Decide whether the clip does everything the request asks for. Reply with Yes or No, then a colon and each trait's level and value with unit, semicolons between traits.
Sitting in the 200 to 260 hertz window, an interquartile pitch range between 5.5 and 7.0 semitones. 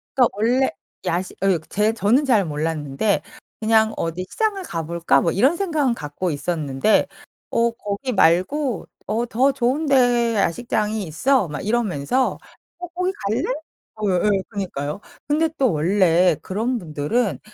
Yes: high, 210 Hz; wide, 6.7 semitones